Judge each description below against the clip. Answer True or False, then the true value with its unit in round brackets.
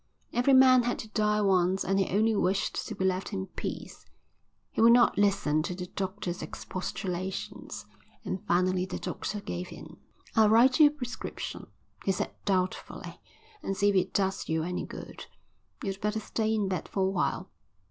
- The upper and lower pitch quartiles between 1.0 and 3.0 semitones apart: True (2.7 semitones)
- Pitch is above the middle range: True (195 Hz)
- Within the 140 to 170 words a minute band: False (180 wpm)